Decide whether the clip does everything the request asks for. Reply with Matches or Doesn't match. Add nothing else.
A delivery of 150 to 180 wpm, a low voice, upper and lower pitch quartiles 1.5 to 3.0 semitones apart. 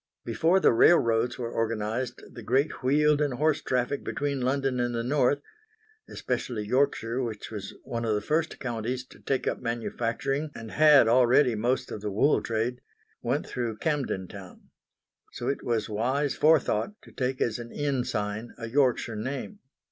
Doesn't match